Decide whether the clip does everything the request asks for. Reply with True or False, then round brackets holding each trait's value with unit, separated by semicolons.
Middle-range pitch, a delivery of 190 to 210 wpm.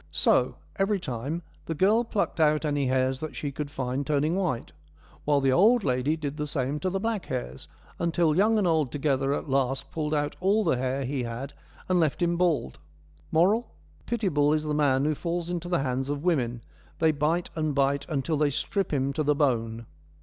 True (150 Hz; 200 wpm)